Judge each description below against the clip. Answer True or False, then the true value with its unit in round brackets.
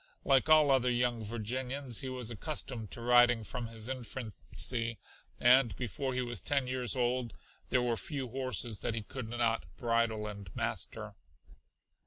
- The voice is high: False (120 Hz)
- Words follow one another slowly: False (155 wpm)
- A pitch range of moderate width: False (2.1 semitones)